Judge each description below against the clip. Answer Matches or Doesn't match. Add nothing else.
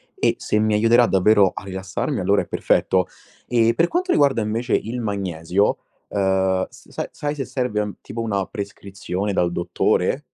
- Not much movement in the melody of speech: Doesn't match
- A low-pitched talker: Matches